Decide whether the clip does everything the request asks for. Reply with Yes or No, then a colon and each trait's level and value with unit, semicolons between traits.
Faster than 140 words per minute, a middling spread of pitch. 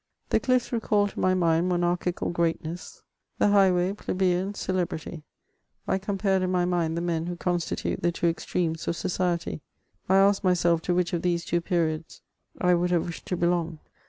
No: average, 180 wpm; narrow, 1.6 semitones